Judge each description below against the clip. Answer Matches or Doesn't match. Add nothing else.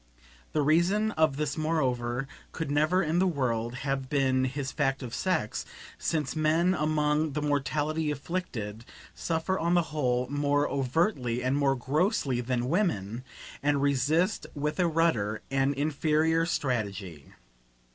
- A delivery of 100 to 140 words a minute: Matches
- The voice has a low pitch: Doesn't match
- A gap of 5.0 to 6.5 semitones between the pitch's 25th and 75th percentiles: Doesn't match